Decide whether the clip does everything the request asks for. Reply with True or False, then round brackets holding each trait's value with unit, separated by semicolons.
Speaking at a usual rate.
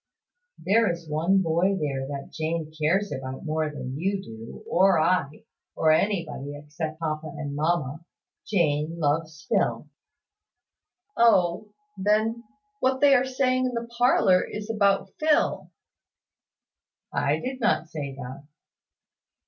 False (125 wpm)